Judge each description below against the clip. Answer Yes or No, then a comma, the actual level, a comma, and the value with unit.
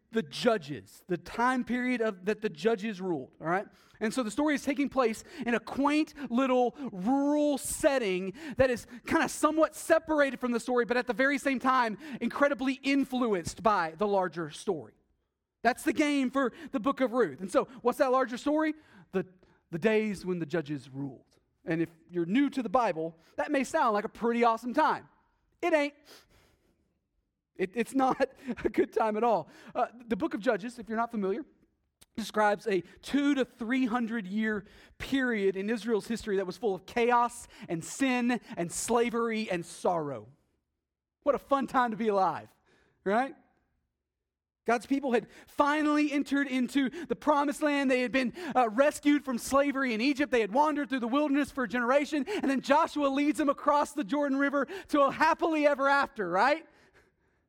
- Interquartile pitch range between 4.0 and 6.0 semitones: Yes, average, 4.6 semitones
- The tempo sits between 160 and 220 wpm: Yes, average, 180 wpm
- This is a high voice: Yes, very high, 250 Hz